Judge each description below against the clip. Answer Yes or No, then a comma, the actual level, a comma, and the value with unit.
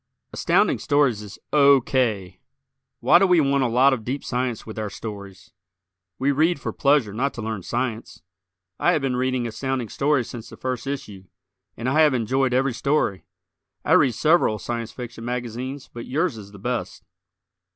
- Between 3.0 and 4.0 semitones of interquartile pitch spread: Yes, average, 3.7 semitones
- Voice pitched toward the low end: Yes, low, 125 Hz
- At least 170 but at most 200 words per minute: Yes, average, 175 wpm